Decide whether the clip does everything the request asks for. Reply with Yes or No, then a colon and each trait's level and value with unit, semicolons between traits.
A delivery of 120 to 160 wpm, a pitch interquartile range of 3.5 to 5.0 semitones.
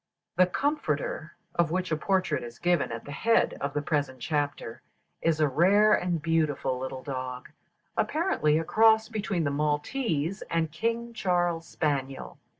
No: average, 155 wpm; wide, 5.5 semitones